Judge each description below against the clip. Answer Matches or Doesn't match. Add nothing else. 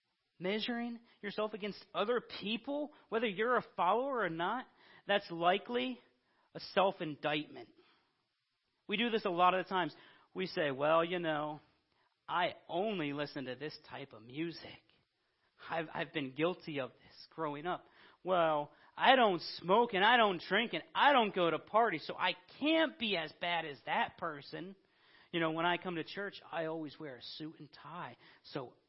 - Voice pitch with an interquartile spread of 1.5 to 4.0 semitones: Doesn't match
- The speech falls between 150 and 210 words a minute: Matches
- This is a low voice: Doesn't match